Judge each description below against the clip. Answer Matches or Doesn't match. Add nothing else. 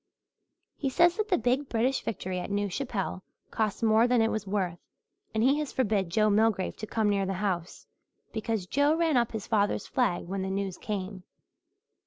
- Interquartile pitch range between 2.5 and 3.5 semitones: Doesn't match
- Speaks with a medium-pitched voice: Doesn't match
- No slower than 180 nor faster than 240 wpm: Matches